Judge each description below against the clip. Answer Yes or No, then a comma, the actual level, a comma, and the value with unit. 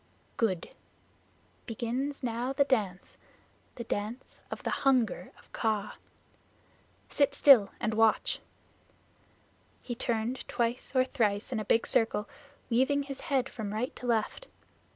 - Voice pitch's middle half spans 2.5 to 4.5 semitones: Yes, average, 3.2 semitones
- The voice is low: No, high, 235 Hz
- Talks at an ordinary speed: No, slow, 130 wpm